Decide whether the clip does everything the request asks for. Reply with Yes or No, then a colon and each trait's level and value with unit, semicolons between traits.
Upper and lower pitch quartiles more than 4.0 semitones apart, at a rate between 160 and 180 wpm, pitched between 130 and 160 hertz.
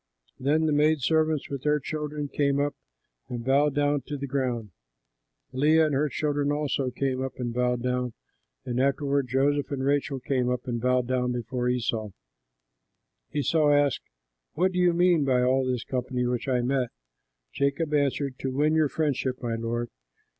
No: average, 2.7 semitones; average, 170 wpm; low, 135 Hz